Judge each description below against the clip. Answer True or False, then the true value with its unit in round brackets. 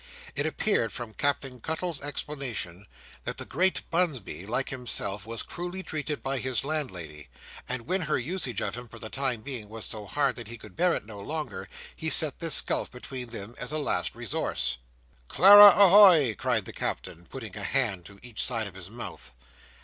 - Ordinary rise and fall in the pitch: False (6.0 semitones)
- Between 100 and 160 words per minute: False (195 wpm)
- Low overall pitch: True (125 Hz)